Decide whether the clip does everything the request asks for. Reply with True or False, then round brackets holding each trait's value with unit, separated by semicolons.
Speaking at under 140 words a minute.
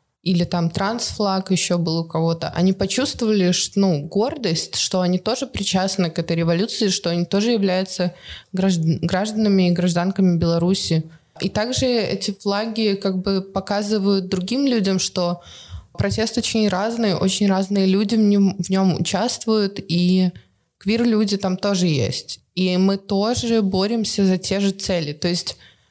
False (145 wpm)